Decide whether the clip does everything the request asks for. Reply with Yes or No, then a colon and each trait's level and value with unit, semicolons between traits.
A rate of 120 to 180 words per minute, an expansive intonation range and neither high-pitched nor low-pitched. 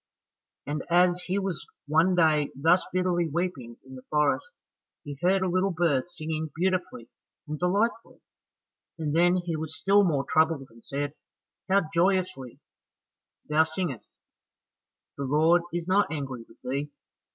No: average, 140 wpm; average, 3.9 semitones; medium, 165 Hz